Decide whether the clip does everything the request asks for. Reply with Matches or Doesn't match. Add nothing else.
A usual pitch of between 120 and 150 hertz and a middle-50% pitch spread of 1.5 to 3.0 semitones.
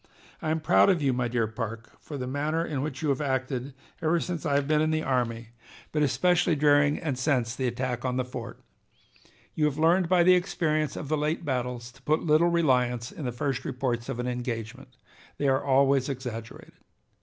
Doesn't match